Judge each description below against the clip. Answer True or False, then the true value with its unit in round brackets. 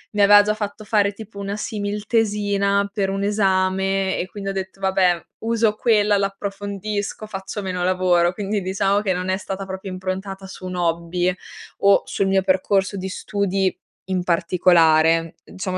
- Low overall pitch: False (195 Hz)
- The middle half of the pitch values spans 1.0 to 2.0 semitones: True (1.5 semitones)